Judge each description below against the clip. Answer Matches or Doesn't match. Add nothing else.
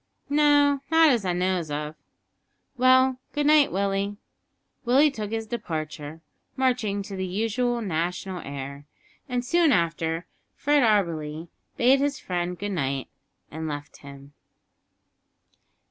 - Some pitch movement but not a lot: Doesn't match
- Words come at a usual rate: Doesn't match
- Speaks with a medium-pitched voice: Doesn't match